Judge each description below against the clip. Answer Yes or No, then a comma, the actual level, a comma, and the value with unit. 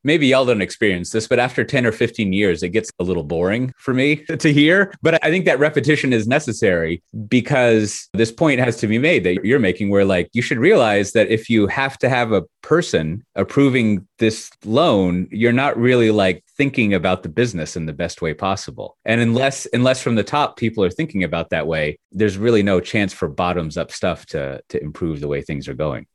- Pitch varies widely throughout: Yes, wide, 6.2 semitones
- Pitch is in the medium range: No, low, 110 Hz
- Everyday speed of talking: No, fast, 215 wpm